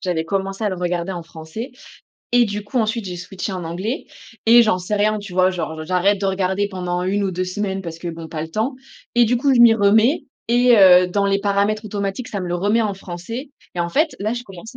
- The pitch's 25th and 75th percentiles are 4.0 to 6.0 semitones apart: No, average, 3.3 semitones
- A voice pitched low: No, high, 195 Hz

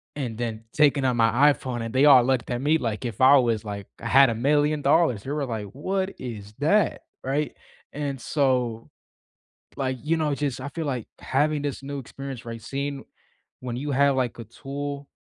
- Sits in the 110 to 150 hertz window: Yes, low, 135 Hz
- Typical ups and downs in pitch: Yes, average, 3.1 semitones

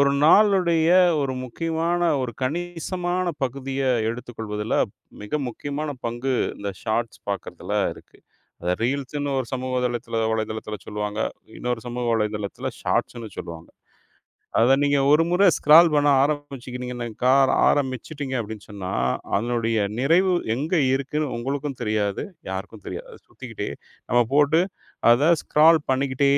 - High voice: No, low, 130 Hz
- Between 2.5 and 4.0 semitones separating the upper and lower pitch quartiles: No, average, 4.6 semitones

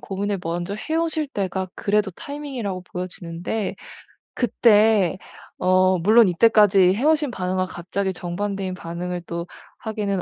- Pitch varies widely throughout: No, average, 3.2 semitones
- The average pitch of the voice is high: Yes, high, 195 Hz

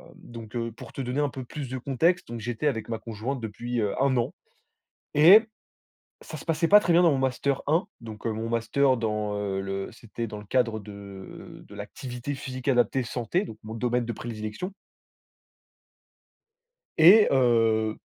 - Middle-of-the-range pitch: No, low, 120 Hz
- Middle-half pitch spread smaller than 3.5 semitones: No, average, 3.8 semitones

